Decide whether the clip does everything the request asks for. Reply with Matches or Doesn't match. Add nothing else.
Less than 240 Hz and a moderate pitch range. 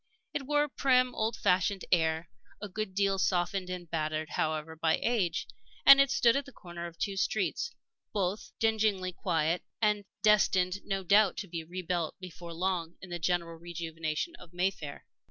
Matches